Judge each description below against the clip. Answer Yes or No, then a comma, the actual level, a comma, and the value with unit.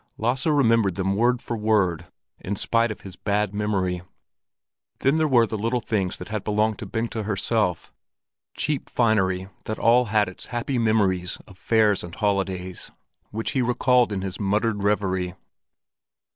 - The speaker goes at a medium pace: Yes, average, 155 wpm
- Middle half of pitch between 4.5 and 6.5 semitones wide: No, average, 3.3 semitones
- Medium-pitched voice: No, low, 105 Hz